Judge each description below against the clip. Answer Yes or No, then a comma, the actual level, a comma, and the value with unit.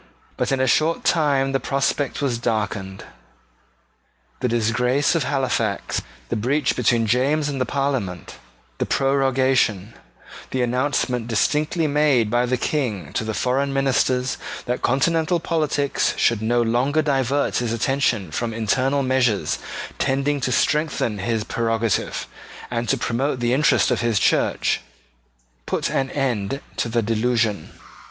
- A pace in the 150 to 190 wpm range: No, slow, 135 wpm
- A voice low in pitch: Yes, low, 125 Hz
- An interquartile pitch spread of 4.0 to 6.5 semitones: No, average, 3.3 semitones